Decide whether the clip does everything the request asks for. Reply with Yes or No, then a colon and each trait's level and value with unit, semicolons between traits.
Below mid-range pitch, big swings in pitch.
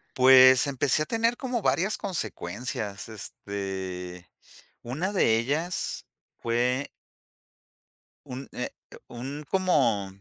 Yes: low, 130 Hz; wide, 6.9 semitones